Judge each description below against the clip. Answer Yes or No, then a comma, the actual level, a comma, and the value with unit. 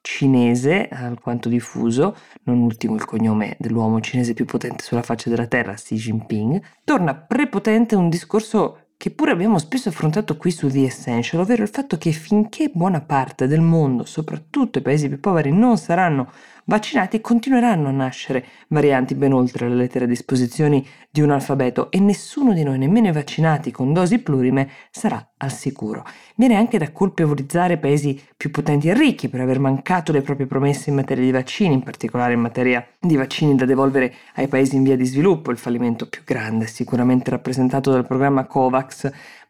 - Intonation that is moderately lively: No, wide, 6.0 semitones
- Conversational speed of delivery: No, fast, 175 wpm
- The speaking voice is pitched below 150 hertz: Yes, medium, 140 Hz